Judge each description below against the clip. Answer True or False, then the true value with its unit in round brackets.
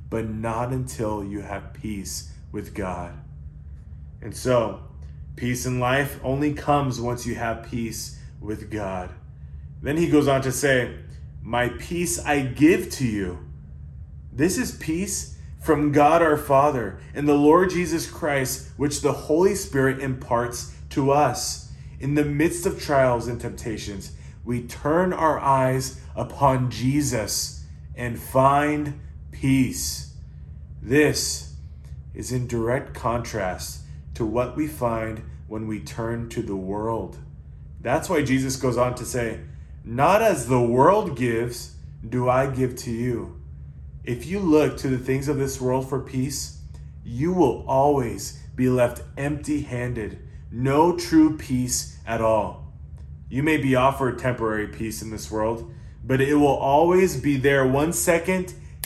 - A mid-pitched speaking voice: False (120 Hz)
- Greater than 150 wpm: False (145 wpm)